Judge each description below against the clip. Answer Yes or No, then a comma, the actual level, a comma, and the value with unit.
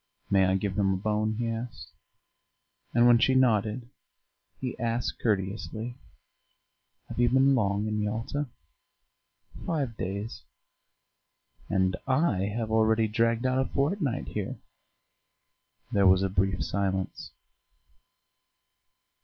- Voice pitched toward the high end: No, low, 110 Hz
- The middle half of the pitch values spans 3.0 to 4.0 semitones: Yes, average, 3.5 semitones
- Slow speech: Yes, slow, 115 wpm